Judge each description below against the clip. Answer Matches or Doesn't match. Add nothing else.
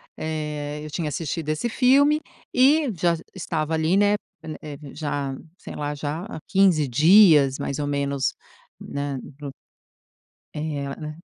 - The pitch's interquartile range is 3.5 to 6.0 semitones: Matches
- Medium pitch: Matches